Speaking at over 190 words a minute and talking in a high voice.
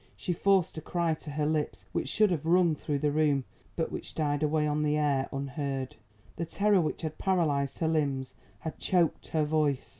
No: average, 200 wpm; medium, 155 Hz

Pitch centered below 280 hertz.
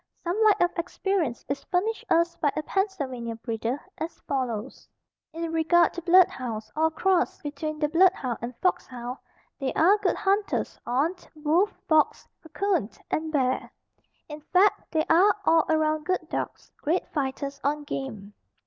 No: very high, 310 Hz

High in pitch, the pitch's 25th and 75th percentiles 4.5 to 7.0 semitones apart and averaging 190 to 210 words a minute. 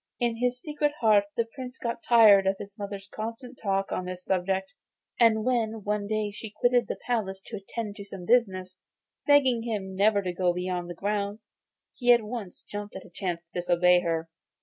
No: high, 205 Hz; average, 3.6 semitones; average, 195 wpm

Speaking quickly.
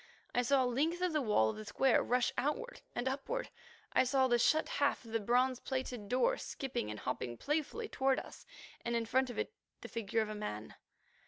Yes: fast, 215 wpm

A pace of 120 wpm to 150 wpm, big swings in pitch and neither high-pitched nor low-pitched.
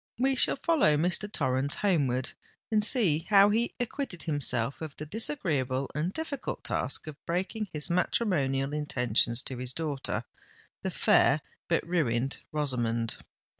Yes: slow, 135 wpm; wide, 7.1 semitones; medium, 150 Hz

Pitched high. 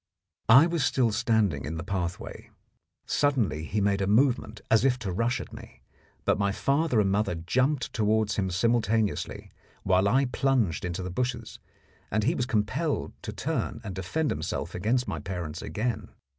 No: low, 110 Hz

